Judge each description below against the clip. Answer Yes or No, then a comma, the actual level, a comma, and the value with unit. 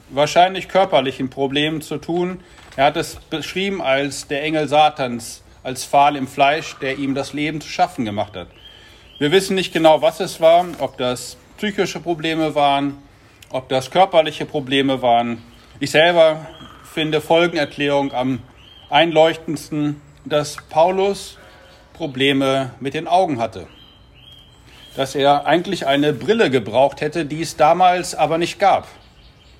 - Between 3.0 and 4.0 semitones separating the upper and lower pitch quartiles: Yes, average, 3.5 semitones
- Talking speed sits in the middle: Yes, average, 140 wpm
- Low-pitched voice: No, medium, 150 Hz